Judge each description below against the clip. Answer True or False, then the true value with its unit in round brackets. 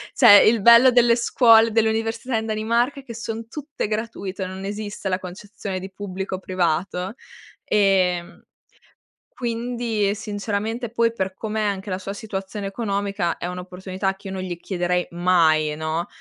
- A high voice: True (200 Hz)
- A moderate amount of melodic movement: True (3.3 semitones)